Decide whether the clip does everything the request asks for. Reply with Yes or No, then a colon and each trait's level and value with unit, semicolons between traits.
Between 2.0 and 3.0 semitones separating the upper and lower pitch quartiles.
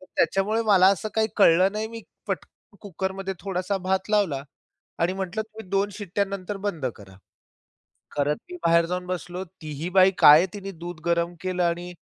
Yes: average, 2.7 semitones